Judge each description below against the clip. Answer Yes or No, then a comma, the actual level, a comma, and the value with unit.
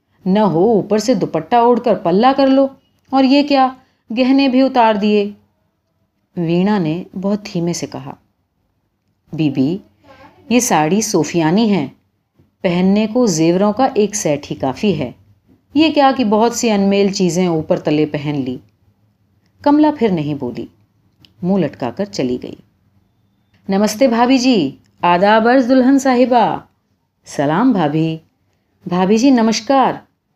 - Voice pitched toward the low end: No, high, 190 Hz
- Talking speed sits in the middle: Yes, average, 135 wpm